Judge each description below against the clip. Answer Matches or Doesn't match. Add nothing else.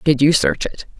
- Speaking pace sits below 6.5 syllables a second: Matches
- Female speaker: Matches